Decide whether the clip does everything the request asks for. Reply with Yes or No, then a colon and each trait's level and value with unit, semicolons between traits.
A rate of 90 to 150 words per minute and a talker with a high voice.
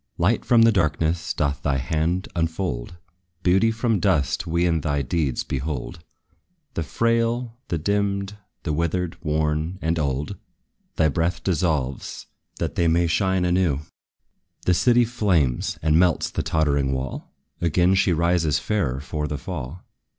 No: average, 145 wpm; very low, 85 Hz